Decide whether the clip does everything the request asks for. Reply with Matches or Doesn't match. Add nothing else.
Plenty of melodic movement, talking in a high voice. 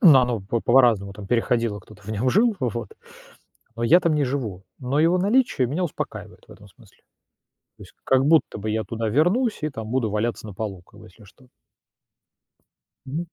Doesn't match